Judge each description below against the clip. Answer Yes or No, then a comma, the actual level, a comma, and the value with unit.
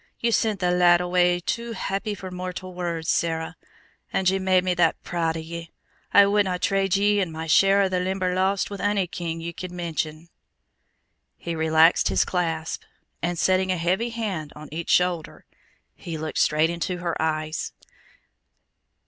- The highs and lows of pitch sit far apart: No, narrow, 2.5 semitones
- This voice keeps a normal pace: Yes, average, 165 wpm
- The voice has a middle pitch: Yes, medium, 180 Hz